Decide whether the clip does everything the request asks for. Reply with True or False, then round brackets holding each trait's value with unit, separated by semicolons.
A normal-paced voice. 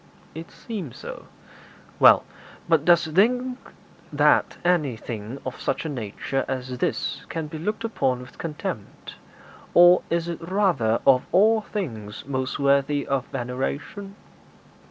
False (130 wpm)